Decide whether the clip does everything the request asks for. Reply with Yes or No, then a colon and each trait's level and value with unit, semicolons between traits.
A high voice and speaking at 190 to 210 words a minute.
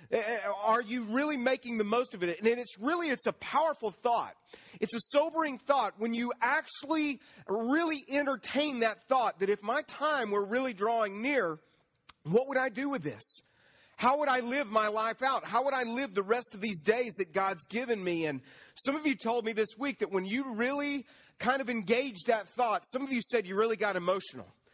Yes: high, 240 Hz; fast, 205 wpm